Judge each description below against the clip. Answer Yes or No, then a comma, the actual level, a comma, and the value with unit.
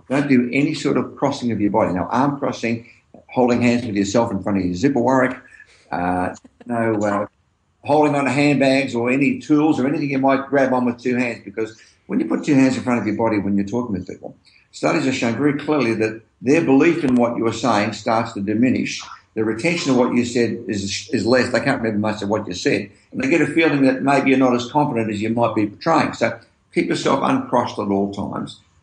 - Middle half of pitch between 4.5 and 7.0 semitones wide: No, average, 3.9 semitones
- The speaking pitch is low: Yes, low, 120 Hz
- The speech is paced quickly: Yes, fast, 235 wpm